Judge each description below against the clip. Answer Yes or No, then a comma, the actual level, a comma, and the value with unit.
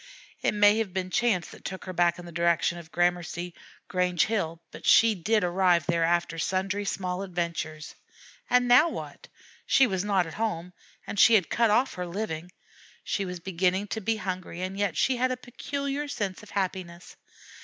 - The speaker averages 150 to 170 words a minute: No, average, 185 wpm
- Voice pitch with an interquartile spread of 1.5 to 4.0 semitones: Yes, average, 3.5 semitones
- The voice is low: No, medium, 185 Hz